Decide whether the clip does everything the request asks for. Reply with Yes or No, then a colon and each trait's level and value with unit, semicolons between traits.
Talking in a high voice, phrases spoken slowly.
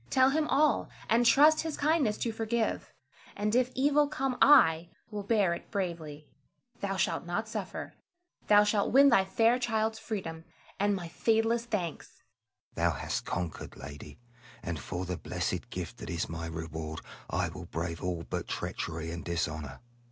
No: high, 200 Hz; average, 165 wpm